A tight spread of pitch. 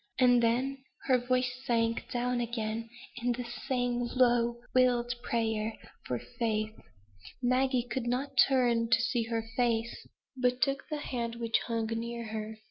Yes: narrow, 1.6 semitones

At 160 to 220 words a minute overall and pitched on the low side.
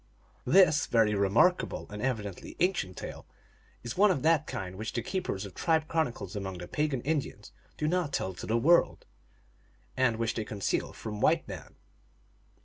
Yes: average, 165 wpm; low, 120 Hz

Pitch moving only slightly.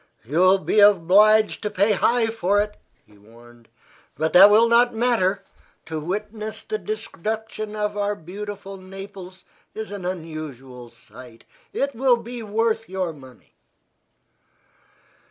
No: average, 4.7 semitones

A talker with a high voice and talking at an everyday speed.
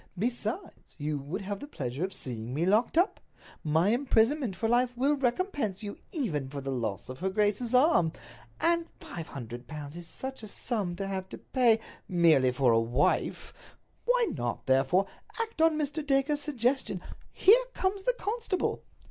Yes: high, 210 Hz; average, 165 wpm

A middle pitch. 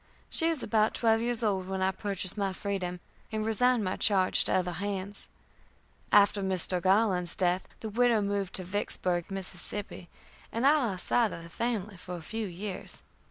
No: high, 200 Hz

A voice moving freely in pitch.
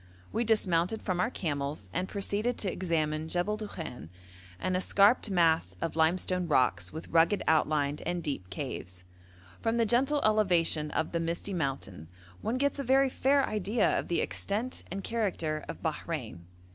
Yes: wide, 5.7 semitones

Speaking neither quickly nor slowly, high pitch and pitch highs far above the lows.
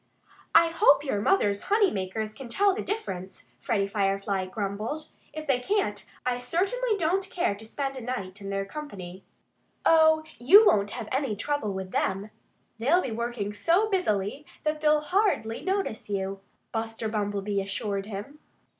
Yes: average, 155 wpm; high, 230 Hz; wide, 7.7 semitones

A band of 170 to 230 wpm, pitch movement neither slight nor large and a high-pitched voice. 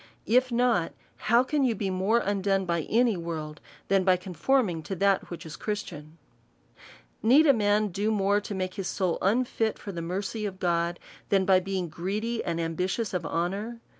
Yes: average, 185 wpm; average, 3.9 semitones; high, 195 Hz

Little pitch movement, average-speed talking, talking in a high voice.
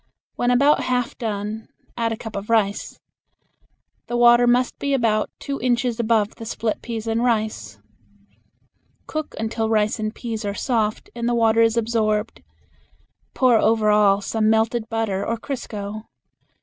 Yes: narrow, 1.9 semitones; average, 150 wpm; high, 225 Hz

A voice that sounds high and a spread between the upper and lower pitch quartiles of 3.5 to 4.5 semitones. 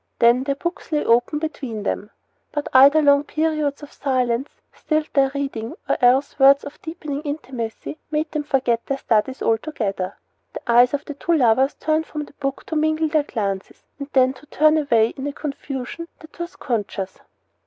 Yes: very high, 280 Hz; average, 3.8 semitones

